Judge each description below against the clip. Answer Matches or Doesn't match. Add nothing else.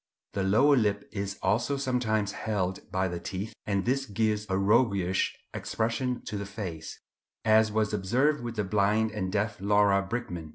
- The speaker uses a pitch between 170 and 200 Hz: Doesn't match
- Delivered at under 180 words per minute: Matches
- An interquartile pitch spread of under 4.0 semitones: Matches